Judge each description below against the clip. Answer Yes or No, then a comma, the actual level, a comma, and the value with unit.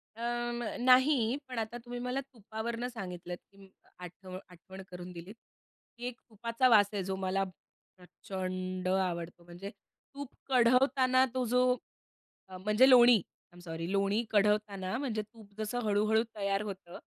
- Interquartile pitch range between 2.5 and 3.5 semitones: No, average, 4.5 semitones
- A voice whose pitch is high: Yes, high, 210 Hz